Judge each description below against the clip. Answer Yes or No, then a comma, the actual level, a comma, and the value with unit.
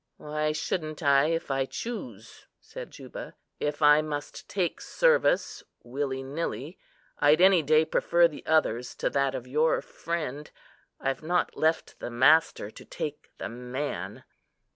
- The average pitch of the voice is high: No, medium, 150 Hz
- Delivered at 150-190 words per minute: No, average, 140 wpm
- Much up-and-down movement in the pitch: No, average, 3.1 semitones